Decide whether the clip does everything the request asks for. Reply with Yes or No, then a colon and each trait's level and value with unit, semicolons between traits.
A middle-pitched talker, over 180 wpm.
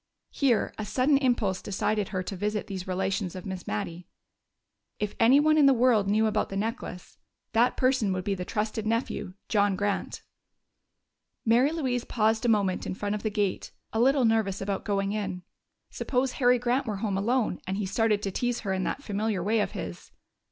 No: high, 210 Hz; average, 190 wpm